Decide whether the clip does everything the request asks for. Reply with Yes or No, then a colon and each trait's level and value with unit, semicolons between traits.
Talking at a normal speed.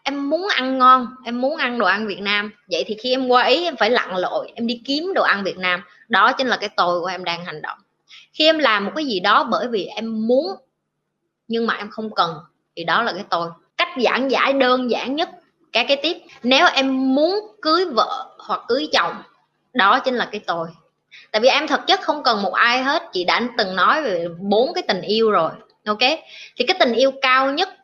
Yes: average, 235 wpm